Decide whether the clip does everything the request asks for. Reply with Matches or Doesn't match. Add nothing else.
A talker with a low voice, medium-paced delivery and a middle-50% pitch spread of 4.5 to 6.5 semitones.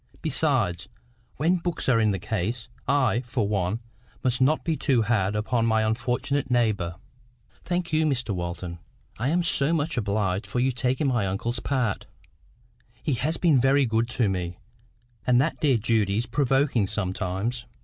Matches